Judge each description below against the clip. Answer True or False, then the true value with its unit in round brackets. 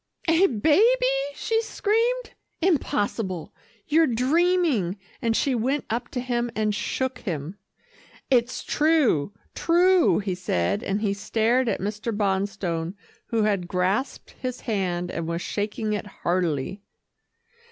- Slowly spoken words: True (125 wpm)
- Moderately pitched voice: False (225 Hz)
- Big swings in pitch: True (6.7 semitones)